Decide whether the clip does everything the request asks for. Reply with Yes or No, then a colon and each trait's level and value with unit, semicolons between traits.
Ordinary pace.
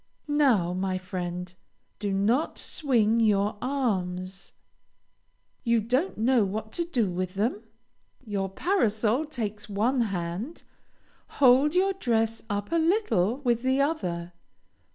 No: slow, 120 wpm